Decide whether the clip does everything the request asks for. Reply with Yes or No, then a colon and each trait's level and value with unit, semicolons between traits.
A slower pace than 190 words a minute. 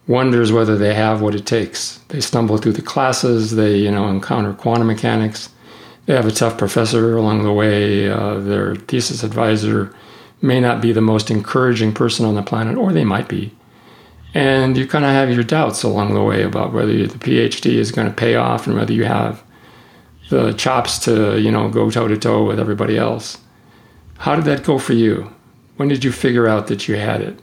No: fast, 205 wpm